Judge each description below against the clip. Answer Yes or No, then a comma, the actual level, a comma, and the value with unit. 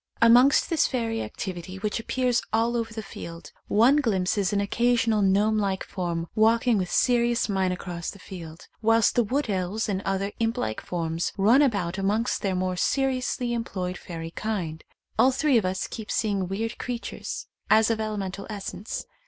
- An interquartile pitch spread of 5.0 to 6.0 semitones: No, average, 3.8 semitones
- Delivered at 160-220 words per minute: Yes, average, 170 wpm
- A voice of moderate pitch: No, high, 210 Hz